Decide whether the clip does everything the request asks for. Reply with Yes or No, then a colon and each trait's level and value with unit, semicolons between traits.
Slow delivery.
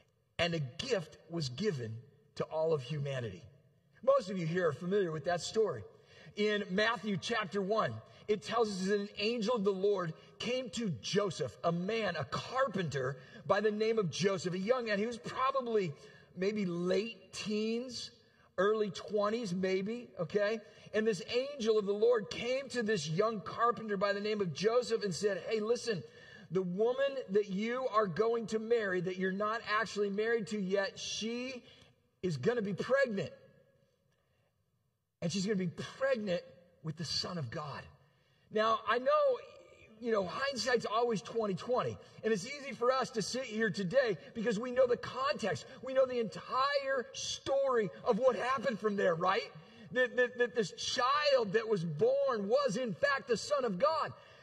No: average, 170 wpm